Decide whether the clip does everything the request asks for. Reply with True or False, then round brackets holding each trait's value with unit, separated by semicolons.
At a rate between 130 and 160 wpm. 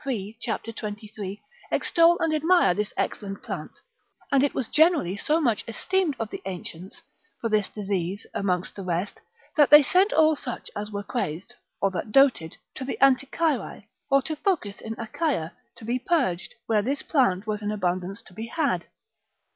False (170 wpm)